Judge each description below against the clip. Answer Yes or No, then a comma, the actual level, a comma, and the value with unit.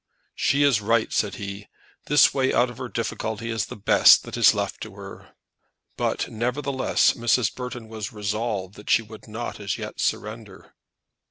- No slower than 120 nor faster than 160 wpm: No, average, 170 wpm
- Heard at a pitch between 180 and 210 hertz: No, low, 115 Hz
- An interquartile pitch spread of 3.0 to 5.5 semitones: No, narrow, 2.6 semitones